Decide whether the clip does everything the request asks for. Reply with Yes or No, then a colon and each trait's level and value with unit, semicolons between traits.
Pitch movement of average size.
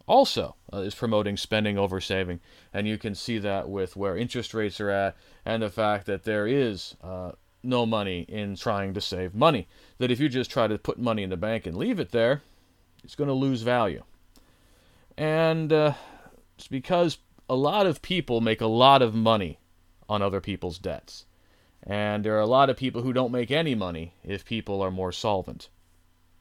Yes: average, 4.8 semitones